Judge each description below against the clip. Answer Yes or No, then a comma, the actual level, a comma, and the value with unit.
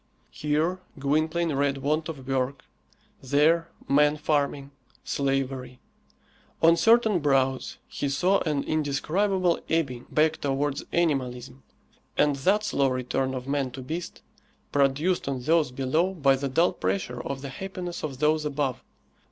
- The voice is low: No, medium, 145 Hz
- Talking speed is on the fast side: No, slow, 135 wpm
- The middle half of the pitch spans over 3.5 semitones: No, average, 3.2 semitones